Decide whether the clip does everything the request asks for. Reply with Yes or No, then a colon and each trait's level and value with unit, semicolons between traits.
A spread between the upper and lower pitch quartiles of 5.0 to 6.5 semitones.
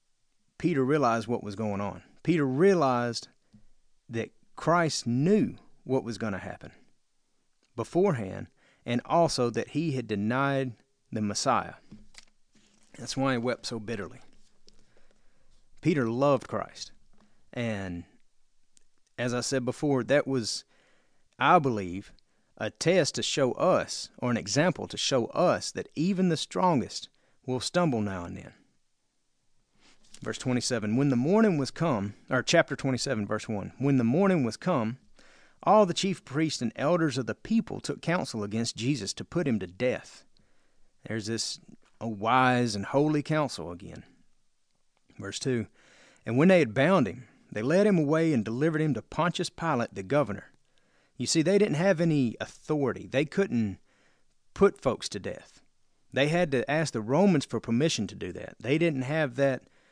Yes: wide, 5.5 semitones